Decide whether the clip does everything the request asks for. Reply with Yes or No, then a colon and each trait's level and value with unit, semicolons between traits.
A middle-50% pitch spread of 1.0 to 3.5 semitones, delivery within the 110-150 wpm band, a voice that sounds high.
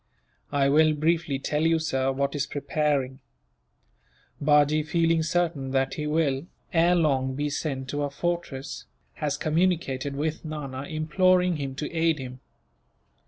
No: average, 2.8 semitones; average, 140 wpm; medium, 150 Hz